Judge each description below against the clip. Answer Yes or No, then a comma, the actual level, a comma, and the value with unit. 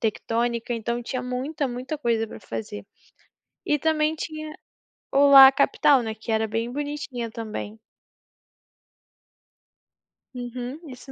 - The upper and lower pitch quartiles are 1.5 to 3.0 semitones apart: No, average, 3.7 semitones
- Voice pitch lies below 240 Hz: No, high, 245 Hz